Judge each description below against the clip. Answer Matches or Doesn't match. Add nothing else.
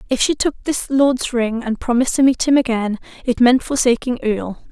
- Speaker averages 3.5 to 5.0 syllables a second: Doesn't match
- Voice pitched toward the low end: Doesn't match